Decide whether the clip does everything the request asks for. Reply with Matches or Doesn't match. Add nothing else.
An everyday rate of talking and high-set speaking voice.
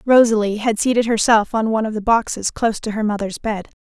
Doesn't match